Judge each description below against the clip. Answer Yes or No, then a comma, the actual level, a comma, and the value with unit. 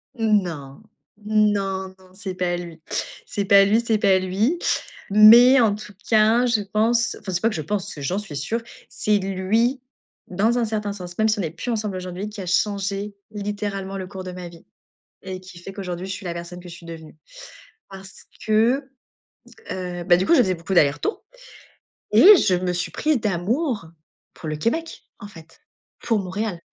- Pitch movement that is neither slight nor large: Yes, average, 3.2 semitones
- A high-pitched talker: Yes, high, 195 Hz